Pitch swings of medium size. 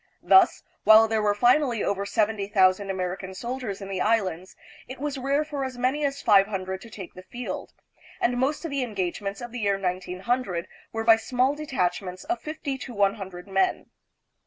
Yes: average, 4.9 semitones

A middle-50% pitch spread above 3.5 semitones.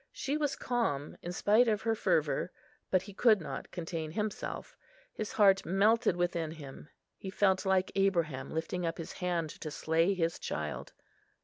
Yes: average, 4.2 semitones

